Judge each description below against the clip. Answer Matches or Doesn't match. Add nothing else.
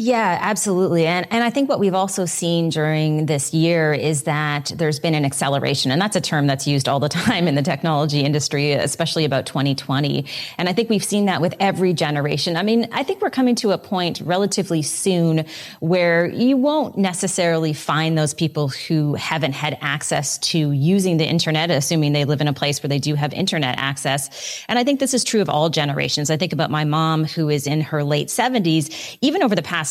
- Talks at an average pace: Doesn't match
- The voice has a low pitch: Doesn't match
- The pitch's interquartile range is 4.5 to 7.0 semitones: Doesn't match